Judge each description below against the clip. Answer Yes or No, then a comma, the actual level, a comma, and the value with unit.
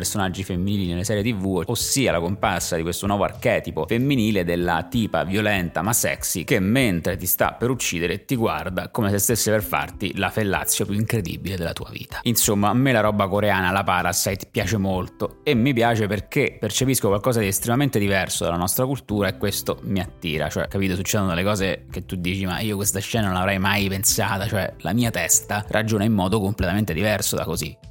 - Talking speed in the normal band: No, fast, 195 wpm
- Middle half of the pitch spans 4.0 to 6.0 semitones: No, average, 3.3 semitones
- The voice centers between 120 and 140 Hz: No, low, 100 Hz